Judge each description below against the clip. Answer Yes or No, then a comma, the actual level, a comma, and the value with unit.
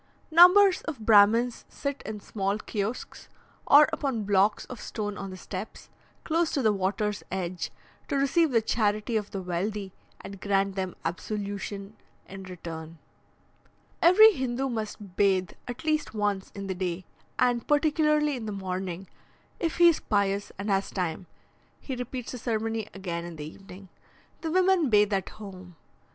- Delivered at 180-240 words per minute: No, average, 155 wpm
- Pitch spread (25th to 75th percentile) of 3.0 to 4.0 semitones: No, average, 4.8 semitones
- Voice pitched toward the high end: Yes, high, 210 Hz